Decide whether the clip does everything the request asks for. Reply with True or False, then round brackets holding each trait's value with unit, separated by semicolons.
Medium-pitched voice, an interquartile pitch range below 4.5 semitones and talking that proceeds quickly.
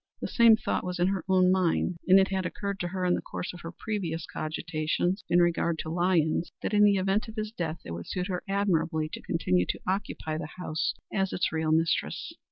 True (180 Hz; 3.0 semitones; 225 wpm)